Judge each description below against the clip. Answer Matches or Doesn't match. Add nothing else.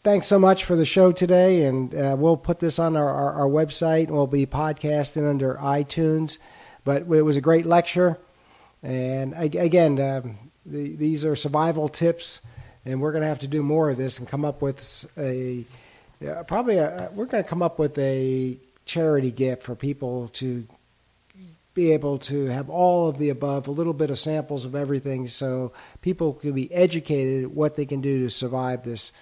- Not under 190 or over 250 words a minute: Matches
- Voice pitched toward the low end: Doesn't match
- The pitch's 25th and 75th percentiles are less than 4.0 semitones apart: Matches